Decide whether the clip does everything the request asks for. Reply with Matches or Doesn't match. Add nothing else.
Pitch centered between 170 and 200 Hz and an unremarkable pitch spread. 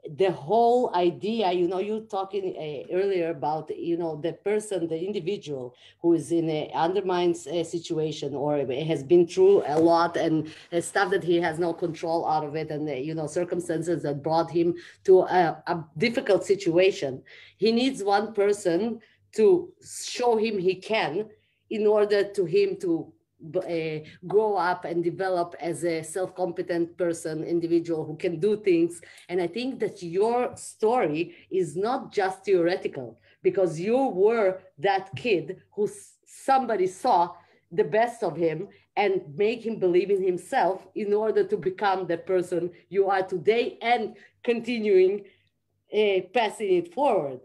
Matches